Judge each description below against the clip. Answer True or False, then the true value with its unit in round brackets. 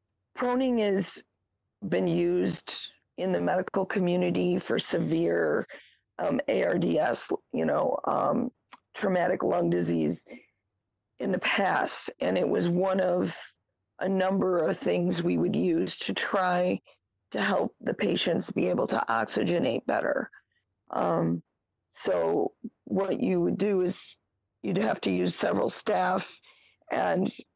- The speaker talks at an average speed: False (125 wpm)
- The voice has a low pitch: False (180 Hz)